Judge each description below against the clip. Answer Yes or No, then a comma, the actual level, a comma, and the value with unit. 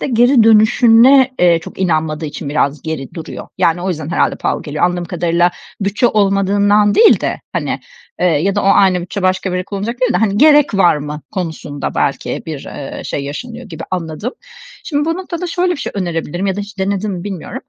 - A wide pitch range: No, average, 5.0 semitones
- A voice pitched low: No, high, 190 Hz